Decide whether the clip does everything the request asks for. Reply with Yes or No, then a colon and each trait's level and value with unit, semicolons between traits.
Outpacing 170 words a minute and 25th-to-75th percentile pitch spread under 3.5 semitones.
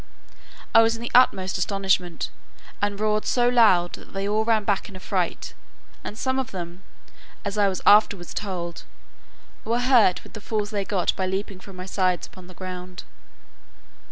Yes: average, 180 wpm; average, 2.7 semitones